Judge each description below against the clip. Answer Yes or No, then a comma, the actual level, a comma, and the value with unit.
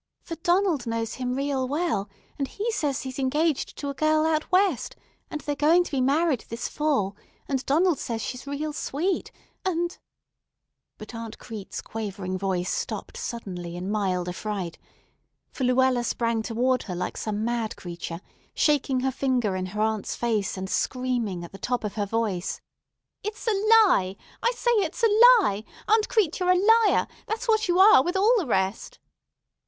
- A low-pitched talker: No, very high, 260 Hz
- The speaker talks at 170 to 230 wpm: Yes, average, 175 wpm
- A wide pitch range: Yes, wide, 8.2 semitones